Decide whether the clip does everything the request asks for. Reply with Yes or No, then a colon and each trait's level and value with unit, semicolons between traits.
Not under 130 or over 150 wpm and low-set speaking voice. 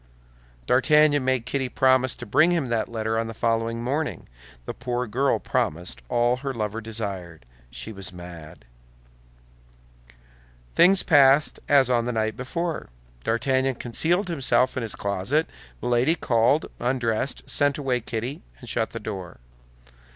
Yes: average, 140 wpm; low, 125 Hz